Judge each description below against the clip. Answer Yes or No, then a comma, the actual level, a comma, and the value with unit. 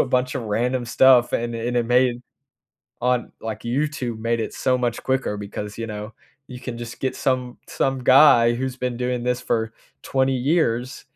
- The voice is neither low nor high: No, low, 125 Hz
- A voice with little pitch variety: Yes, narrow, 1.8 semitones